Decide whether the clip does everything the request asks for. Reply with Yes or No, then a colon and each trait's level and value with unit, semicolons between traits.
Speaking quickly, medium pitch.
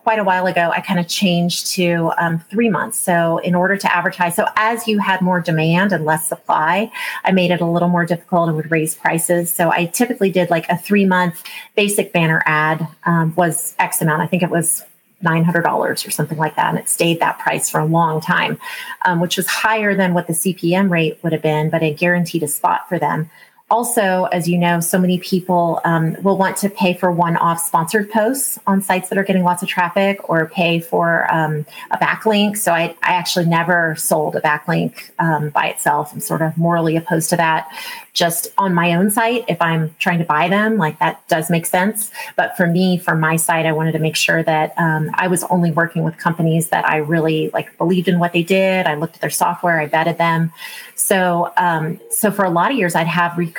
Yes: fast, 225 wpm; medium, 175 Hz